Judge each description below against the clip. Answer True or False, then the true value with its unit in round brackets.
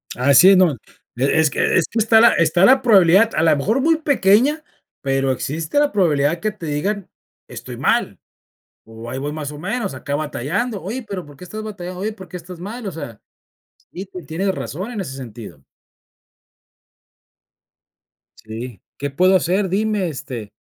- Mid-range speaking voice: True (180 Hz)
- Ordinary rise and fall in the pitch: False (6.4 semitones)